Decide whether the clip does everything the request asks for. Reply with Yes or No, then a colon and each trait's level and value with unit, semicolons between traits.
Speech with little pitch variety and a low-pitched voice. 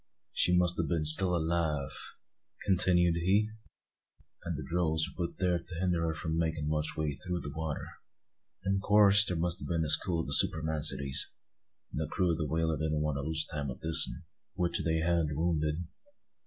Yes: narrow, 2.2 semitones; very low, 80 Hz